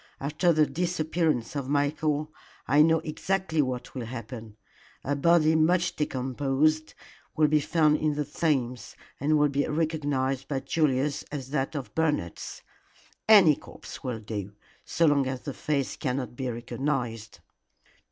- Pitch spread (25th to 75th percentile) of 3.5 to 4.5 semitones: No, average, 3.1 semitones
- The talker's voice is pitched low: No, medium, 145 Hz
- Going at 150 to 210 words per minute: No, average, 140 wpm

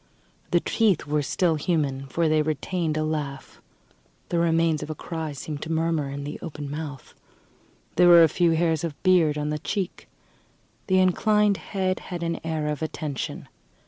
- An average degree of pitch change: No, narrow, 2.3 semitones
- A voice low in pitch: No, medium, 160 Hz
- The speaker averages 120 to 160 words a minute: No, average, 175 wpm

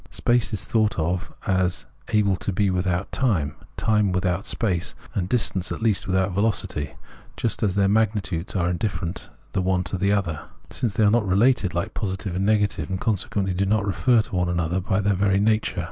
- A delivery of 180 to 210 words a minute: Yes, average, 195 wpm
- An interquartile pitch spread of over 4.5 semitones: No, average, 2.8 semitones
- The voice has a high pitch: No, very low, 95 Hz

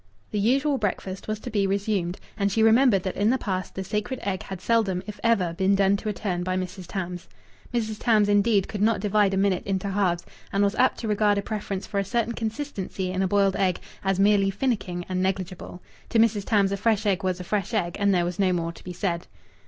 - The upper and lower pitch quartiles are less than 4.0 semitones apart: Yes, narrow, 2.4 semitones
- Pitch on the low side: No, high, 200 Hz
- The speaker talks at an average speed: No, fast, 235 wpm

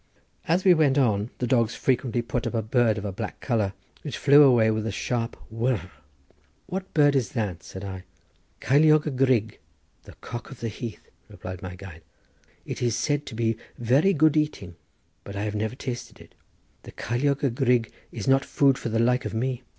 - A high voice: No, low, 120 Hz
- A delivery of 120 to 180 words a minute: No, average, 195 wpm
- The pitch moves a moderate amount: Yes, average, 3.9 semitones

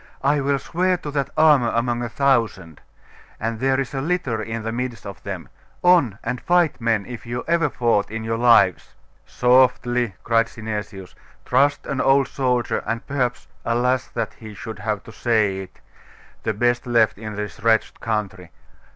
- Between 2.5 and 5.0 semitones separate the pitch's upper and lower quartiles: Yes, average, 3.3 semitones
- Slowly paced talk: No, average, 170 wpm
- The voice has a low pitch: Yes, low, 120 Hz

